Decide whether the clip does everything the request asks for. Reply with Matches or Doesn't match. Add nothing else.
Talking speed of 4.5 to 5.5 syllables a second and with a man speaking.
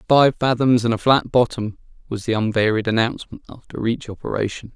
Doesn't match